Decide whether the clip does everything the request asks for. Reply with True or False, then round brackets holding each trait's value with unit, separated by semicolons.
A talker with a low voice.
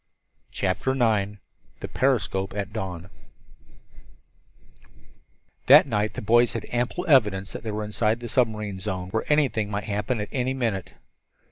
True (110 Hz)